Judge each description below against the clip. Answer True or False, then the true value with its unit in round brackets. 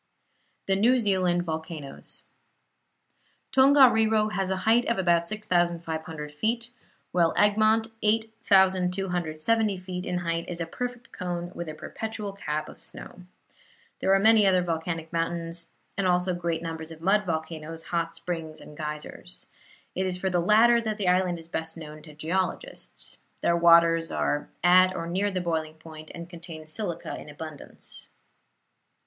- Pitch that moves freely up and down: False (3.4 semitones)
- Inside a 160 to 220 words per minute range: False (150 wpm)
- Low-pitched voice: False (175 Hz)